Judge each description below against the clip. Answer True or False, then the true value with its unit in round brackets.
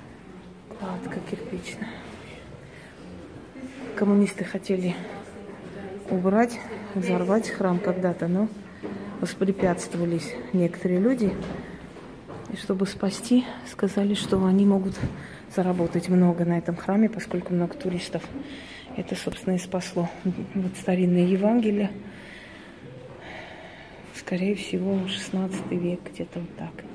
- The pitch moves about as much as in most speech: False (2.1 semitones)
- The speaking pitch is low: False (190 Hz)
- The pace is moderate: False (90 wpm)